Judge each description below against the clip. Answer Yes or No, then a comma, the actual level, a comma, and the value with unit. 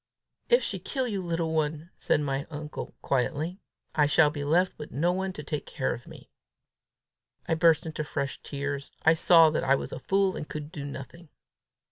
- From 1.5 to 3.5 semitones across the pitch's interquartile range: Yes, average, 2.8 semitones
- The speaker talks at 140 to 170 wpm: No, average, 185 wpm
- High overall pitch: No, medium, 155 Hz